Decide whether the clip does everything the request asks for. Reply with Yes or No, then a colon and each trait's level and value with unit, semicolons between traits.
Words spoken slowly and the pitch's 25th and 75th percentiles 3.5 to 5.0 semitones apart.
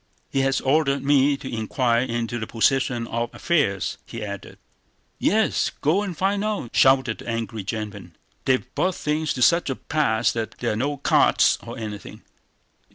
No: average, 165 wpm; average, 4.4 semitones